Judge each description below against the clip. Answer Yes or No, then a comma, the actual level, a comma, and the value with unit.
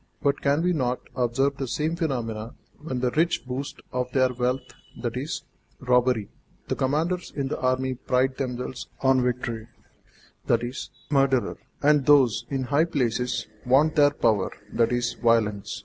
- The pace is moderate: Yes, average, 145 wpm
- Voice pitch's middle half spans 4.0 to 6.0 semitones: No, narrow, 2.5 semitones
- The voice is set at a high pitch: No, low, 130 Hz